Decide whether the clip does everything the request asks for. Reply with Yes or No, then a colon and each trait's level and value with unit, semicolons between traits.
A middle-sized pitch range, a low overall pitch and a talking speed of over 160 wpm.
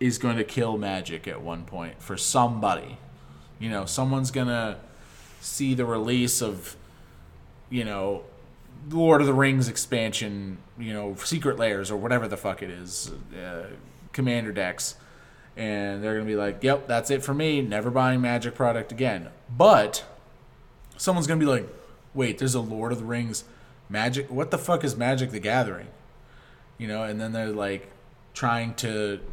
Yes: average, 3.8 semitones; low, 120 Hz; average, 170 wpm